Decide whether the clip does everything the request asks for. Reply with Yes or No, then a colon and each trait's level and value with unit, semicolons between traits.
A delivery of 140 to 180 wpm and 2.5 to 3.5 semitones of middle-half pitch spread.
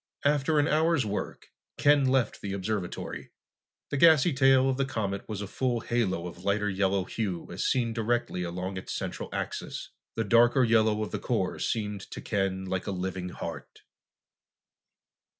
No: average, 165 wpm; average, 5.3 semitones